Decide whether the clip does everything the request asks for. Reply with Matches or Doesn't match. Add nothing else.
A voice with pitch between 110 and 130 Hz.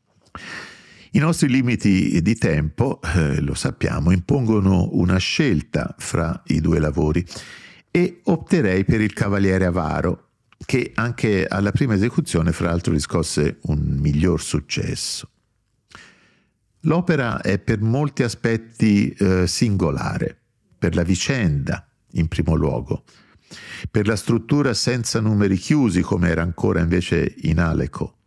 Doesn't match